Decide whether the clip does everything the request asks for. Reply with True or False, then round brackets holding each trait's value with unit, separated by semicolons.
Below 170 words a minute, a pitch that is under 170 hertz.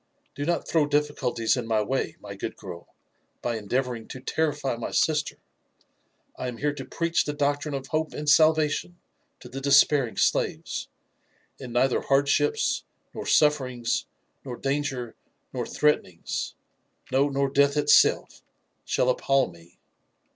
True (145 wpm; 135 Hz)